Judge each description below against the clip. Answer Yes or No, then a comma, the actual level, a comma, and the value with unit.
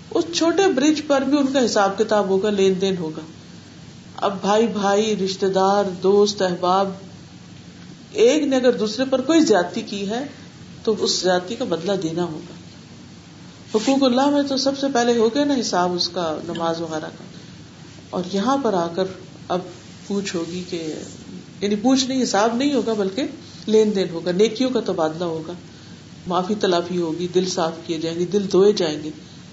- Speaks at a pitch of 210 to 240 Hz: No, high, 195 Hz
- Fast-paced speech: No, average, 175 wpm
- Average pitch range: Yes, average, 5.0 semitones